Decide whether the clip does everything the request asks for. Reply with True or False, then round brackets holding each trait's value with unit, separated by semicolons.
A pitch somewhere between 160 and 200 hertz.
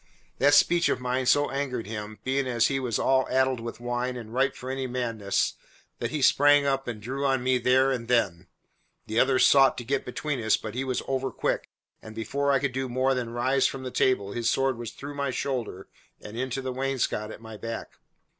False (130 Hz)